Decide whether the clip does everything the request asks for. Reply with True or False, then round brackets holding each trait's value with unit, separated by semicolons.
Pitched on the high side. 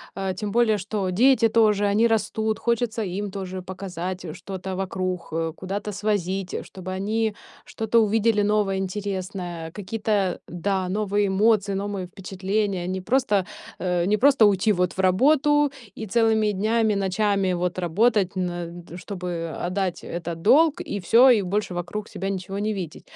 True (195 Hz)